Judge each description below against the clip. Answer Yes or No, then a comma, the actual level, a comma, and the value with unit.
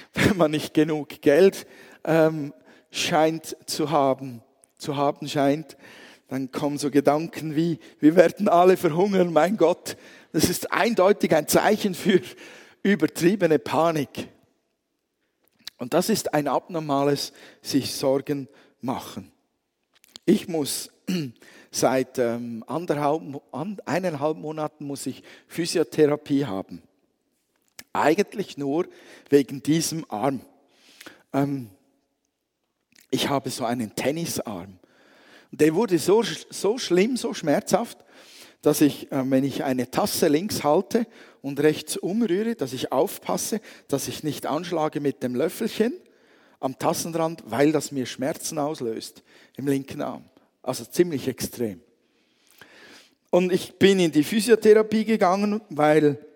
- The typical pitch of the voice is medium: Yes, medium, 155 Hz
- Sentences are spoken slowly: Yes, slow, 115 wpm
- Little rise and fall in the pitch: No, average, 4.5 semitones